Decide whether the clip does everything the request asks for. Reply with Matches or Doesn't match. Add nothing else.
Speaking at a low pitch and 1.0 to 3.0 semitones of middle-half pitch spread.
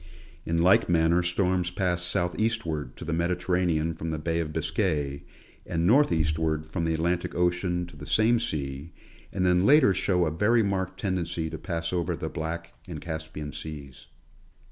Matches